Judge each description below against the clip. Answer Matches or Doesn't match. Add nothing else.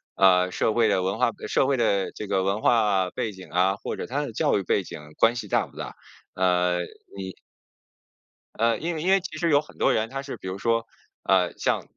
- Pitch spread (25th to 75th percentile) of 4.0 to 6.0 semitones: Matches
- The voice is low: Matches